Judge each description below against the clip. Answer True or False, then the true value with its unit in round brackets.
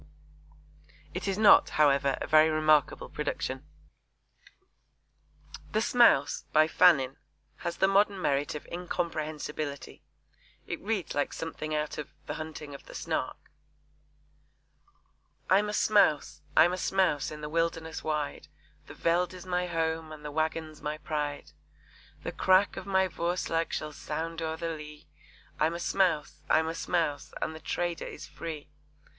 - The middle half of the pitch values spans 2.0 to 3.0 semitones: True (2.6 semitones)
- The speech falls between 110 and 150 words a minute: True (145 wpm)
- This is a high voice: False (160 Hz)